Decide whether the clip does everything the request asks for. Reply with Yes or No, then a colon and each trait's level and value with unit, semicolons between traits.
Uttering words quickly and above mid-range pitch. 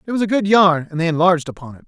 No: fast, 320 wpm; medium, 175 Hz